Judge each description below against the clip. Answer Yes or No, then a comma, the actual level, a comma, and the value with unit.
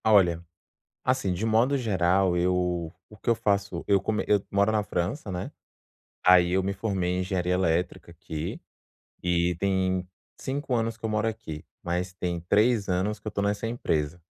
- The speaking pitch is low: Yes, very low, 95 Hz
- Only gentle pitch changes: No, average, 3.3 semitones